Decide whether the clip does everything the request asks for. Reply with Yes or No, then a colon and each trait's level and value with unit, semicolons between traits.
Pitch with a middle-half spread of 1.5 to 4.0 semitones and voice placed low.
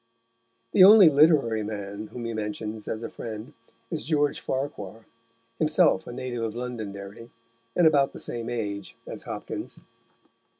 No: average, 5.0 semitones; low, 115 Hz